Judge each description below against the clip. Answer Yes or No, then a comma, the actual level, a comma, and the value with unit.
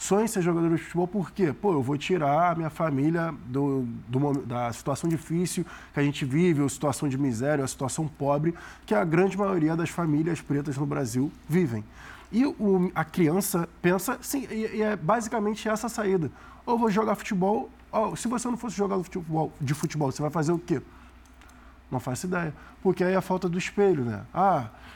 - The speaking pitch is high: No, medium, 165 Hz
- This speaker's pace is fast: Yes, fast, 200 wpm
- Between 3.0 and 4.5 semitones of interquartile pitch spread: No, average, 5.0 semitones